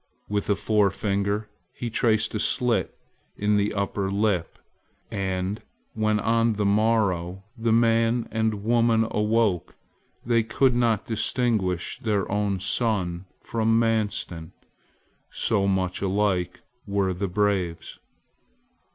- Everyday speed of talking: No, slow, 115 wpm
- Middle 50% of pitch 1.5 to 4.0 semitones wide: Yes, narrow, 2.5 semitones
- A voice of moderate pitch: No, low, 105 Hz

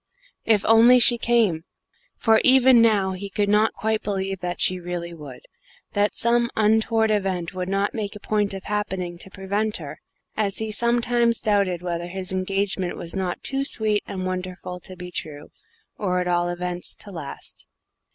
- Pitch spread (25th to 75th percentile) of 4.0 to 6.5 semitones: No, average, 3.4 semitones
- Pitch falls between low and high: No, high, 195 Hz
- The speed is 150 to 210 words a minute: Yes, average, 170 wpm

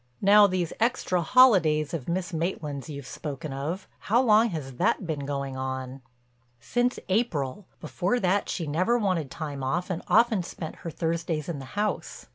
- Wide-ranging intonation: Yes, wide, 5.7 semitones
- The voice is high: No, medium, 165 Hz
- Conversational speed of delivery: Yes, average, 160 wpm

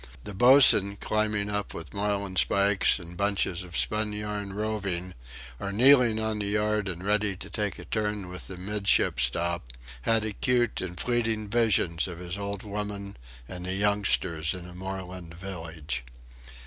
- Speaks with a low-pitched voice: Yes, low, 100 Hz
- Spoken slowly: No, average, 150 wpm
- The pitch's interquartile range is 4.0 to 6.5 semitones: No, average, 2.7 semitones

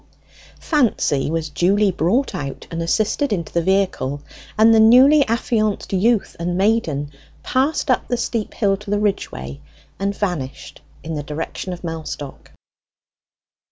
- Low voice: No, high, 195 Hz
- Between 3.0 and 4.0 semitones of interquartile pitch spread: No, wide, 5.5 semitones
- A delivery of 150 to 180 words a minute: No, average, 140 wpm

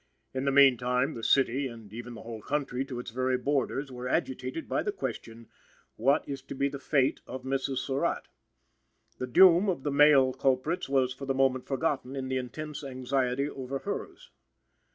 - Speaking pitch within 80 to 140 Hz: Yes, low, 135 Hz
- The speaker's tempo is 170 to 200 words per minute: Yes, average, 180 wpm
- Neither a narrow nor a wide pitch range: No, narrow, 1.7 semitones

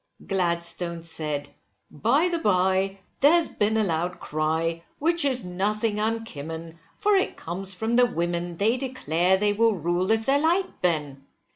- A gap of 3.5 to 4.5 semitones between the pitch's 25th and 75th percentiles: No, wide, 5.4 semitones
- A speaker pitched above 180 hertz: Yes, high, 190 Hz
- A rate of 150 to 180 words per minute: Yes, average, 155 wpm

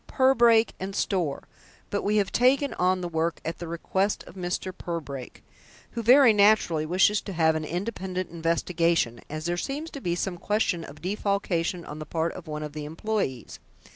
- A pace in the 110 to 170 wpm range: No, average, 180 wpm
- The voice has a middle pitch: Yes, medium, 180 Hz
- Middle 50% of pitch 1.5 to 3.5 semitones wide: No, average, 4.1 semitones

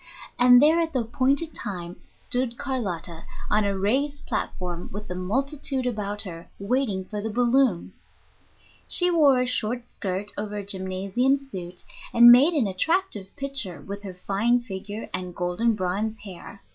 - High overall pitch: Yes, high, 215 Hz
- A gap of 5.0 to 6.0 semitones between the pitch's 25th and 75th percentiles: Yes, wide, 5.5 semitones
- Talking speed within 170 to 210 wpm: No, average, 155 wpm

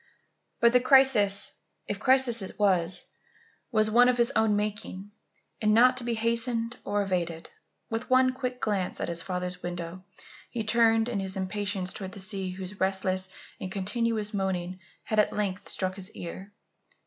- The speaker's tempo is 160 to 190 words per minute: Yes, average, 165 wpm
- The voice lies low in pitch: No, high, 205 Hz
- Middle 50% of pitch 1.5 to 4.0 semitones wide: Yes, average, 3.6 semitones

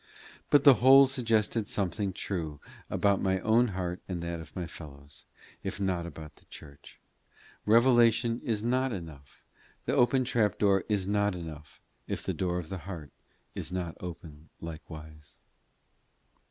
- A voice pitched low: Yes, very low, 95 Hz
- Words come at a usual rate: Yes, average, 150 wpm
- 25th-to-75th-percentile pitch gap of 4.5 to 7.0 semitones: Yes, wide, 5.5 semitones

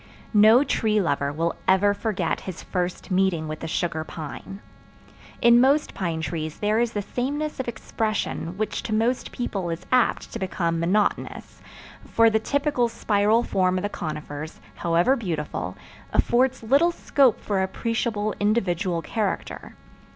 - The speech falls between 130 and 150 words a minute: Yes, average, 145 wpm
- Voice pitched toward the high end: Yes, high, 205 Hz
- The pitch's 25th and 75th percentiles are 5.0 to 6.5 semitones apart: Yes, wide, 5.5 semitones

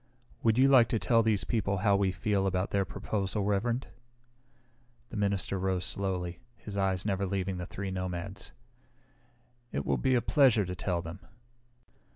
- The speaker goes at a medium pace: Yes, average, 165 wpm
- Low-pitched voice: Yes, low, 100 Hz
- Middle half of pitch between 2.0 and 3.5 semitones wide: Yes, narrow, 2.6 semitones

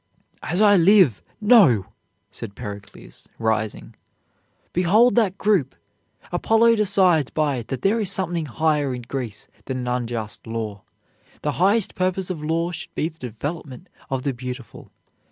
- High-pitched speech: No, medium, 155 Hz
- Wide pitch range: Yes, wide, 7.4 semitones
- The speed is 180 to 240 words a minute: No, average, 145 wpm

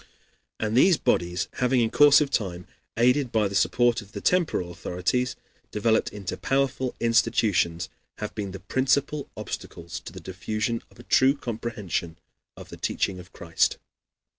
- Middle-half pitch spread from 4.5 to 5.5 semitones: Yes, average, 5.2 semitones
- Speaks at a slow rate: No, average, 155 wpm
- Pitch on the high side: No, low, 110 Hz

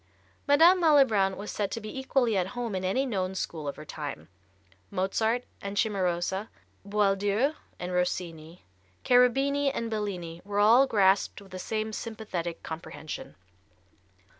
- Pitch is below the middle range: No, high, 200 Hz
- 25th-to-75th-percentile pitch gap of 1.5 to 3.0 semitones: No, average, 4.2 semitones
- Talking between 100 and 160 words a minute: Yes, average, 140 wpm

